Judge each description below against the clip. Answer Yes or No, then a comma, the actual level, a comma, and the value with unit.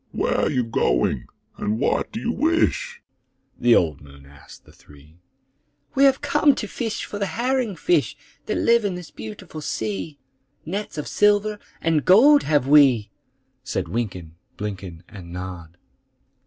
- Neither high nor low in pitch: Yes, medium, 150 Hz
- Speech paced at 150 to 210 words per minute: Yes, average, 155 wpm